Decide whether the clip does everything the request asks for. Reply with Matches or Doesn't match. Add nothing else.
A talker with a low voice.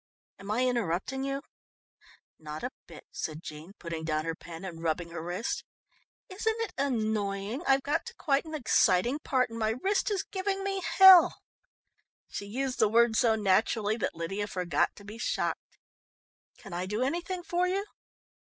Doesn't match